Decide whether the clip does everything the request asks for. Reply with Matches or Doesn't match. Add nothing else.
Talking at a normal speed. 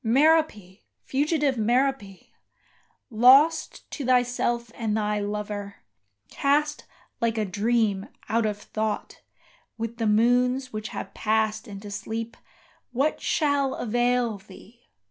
Doesn't match